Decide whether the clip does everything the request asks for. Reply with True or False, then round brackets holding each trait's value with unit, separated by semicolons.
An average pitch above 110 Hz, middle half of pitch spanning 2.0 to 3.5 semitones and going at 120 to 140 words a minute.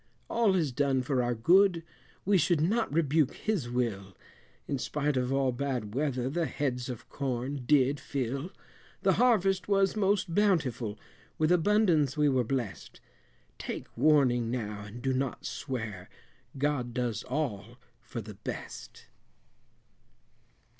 False (135 Hz; 5.0 semitones; 135 wpm)